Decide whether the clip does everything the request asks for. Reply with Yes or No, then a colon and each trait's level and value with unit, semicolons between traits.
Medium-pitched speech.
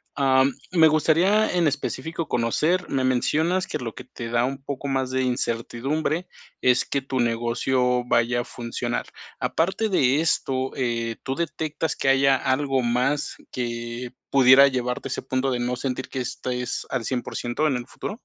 No: low, 130 Hz